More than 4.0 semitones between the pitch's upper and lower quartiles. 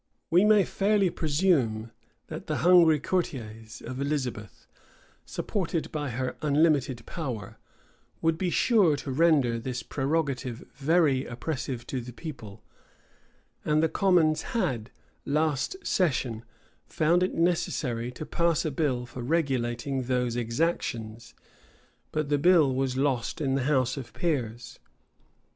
Yes: average, 4.9 semitones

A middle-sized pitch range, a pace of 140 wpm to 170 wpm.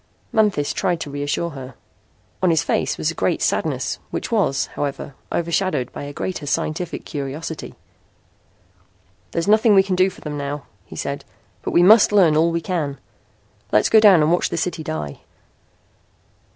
Yes: average, 4.5 semitones; average, 165 wpm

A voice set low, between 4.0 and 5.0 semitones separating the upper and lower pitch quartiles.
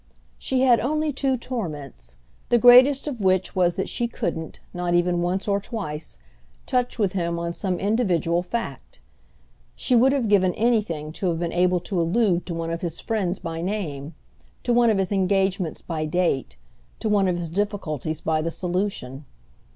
No: medium, 185 Hz; average, 4.7 semitones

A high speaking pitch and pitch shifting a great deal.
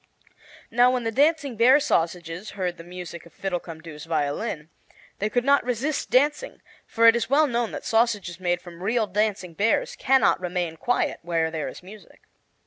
Yes: high, 205 Hz; wide, 6.1 semitones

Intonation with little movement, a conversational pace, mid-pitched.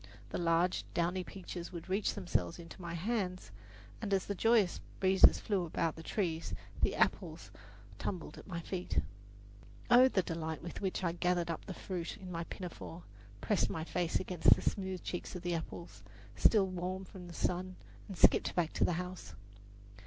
Yes: narrow, 2.0 semitones; average, 175 wpm; medium, 180 Hz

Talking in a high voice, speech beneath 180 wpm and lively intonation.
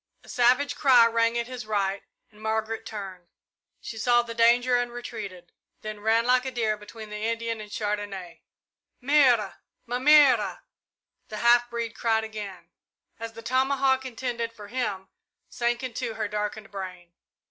No: high, 230 Hz; average, 155 wpm; narrow, 2.5 semitones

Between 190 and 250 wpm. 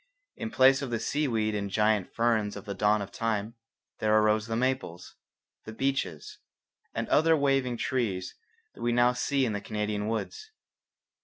No: average, 170 wpm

